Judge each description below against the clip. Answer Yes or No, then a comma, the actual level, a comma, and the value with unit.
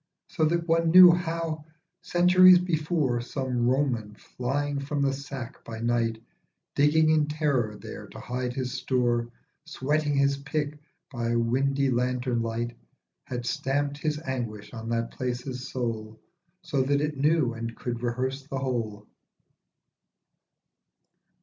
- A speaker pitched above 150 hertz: No, low, 135 Hz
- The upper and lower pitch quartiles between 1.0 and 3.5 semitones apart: No, average, 3.9 semitones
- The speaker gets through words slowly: Yes, slow, 130 wpm